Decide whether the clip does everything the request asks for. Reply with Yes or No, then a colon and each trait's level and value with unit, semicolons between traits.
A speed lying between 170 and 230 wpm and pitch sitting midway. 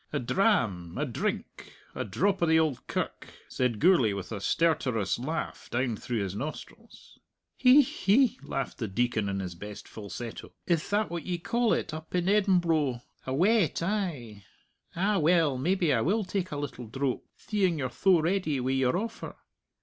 Yes: average, 175 wpm; medium, 155 Hz